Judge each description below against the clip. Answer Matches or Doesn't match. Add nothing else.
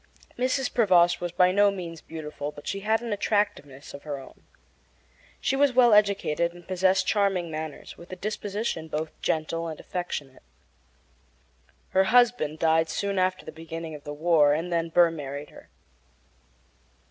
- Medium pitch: Matches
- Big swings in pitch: Doesn't match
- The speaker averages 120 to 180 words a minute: Matches